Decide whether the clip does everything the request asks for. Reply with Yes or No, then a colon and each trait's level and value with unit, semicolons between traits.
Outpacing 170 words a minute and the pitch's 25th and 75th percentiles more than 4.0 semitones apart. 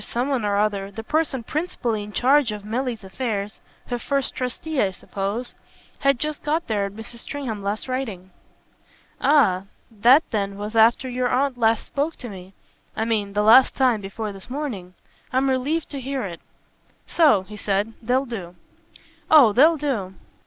No: average, 165 wpm; average, 4.7 semitones